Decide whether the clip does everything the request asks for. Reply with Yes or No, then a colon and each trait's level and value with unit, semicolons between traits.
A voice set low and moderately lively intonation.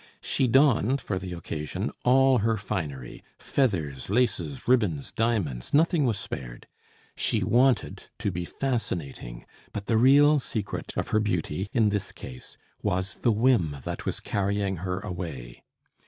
No: low, 105 Hz; wide, 6.5 semitones